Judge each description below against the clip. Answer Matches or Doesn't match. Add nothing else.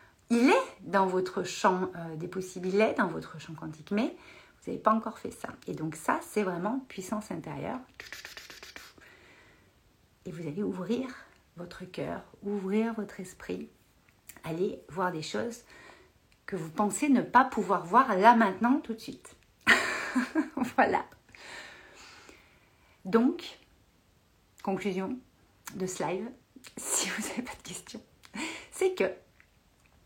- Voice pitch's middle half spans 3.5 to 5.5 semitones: Matches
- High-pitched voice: Matches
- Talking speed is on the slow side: Matches